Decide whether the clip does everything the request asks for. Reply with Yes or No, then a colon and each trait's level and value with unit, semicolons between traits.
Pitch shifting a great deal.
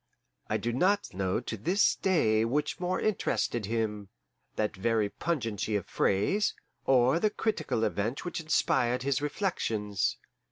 Yes: wide, 8.0 semitones